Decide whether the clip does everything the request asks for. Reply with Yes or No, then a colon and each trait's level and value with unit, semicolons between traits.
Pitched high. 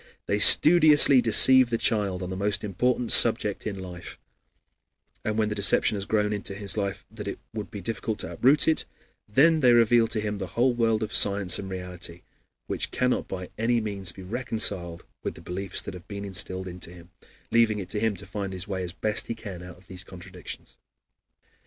No: low, 105 Hz